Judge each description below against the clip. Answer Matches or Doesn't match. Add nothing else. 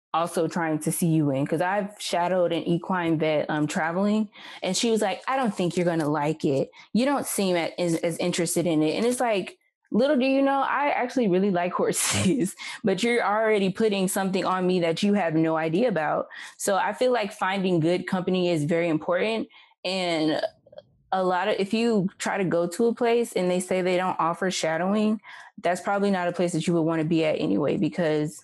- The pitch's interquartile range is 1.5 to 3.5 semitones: Doesn't match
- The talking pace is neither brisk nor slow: Doesn't match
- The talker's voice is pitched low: Doesn't match